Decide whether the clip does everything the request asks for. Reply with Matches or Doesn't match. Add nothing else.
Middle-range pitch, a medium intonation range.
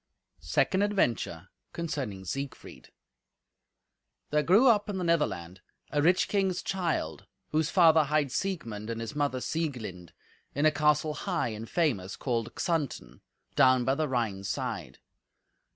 Doesn't match